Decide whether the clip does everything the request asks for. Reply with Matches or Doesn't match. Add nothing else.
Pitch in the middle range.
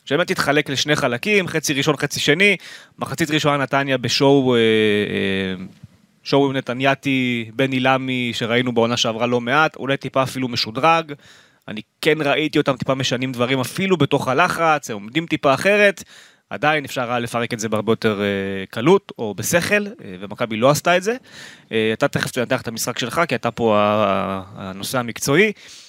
Doesn't match